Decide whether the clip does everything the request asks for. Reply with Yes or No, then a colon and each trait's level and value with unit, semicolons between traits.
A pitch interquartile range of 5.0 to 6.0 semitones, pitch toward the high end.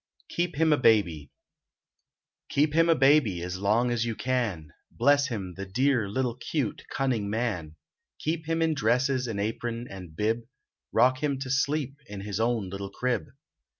No: wide, 5.6 semitones; low, 120 Hz